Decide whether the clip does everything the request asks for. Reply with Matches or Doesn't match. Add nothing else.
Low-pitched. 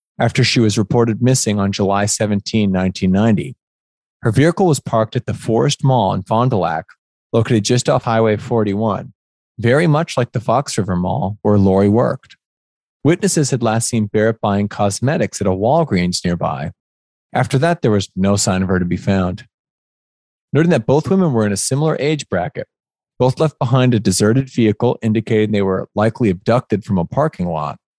Matches